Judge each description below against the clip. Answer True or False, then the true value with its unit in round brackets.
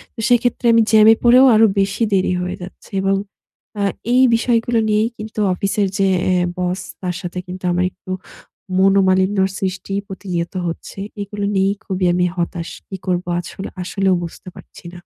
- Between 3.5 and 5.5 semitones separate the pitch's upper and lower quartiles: False (2.7 semitones)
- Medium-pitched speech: False (195 Hz)